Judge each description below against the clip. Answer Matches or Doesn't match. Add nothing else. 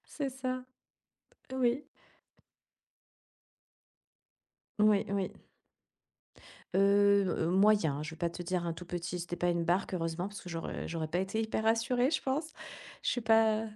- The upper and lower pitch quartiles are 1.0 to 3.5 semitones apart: Doesn't match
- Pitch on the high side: Matches